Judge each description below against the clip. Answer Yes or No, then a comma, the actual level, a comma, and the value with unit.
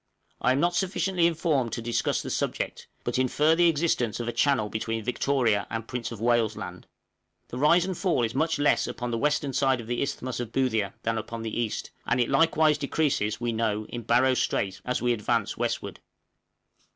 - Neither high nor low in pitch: No, low, 125 Hz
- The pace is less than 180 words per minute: No, average, 200 wpm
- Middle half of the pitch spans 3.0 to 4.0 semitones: No, average, 4.5 semitones